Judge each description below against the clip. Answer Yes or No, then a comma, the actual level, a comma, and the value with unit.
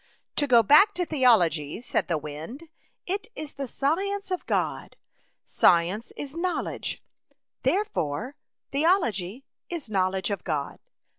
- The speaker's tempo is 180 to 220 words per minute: No, average, 140 wpm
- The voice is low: No, very high, 260 Hz